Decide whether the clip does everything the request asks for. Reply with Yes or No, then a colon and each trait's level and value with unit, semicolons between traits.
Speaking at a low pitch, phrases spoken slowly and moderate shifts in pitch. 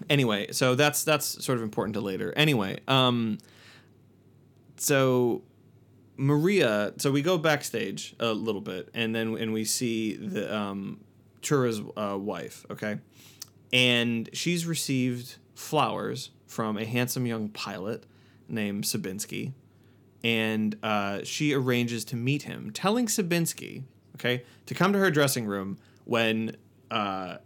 Yes: low, 120 Hz; slow, 130 wpm; average, 3.6 semitones